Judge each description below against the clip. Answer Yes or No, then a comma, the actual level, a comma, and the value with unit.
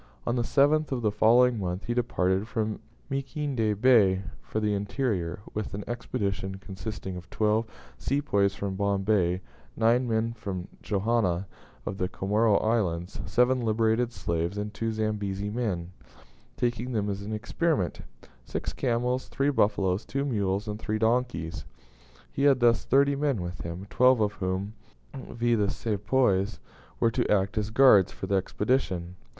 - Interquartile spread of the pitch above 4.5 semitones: No, average, 3.8 semitones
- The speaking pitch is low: Yes, low, 105 Hz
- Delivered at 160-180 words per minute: No, average, 150 wpm